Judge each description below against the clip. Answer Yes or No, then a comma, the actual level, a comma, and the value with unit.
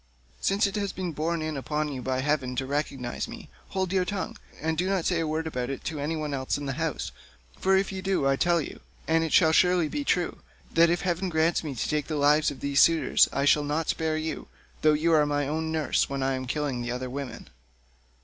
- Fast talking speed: Yes, fast, 235 wpm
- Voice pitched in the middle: Yes, medium, 155 Hz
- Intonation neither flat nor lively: Yes, average, 3.2 semitones